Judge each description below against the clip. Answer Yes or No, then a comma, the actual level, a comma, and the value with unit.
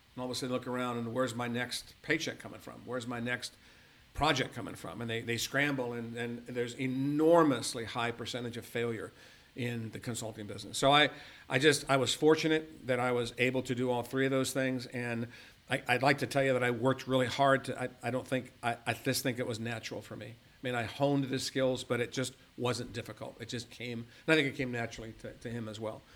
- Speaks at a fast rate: Yes, fast, 240 wpm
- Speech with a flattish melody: Yes, narrow, 2.0 semitones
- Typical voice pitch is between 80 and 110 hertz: No, low, 125 Hz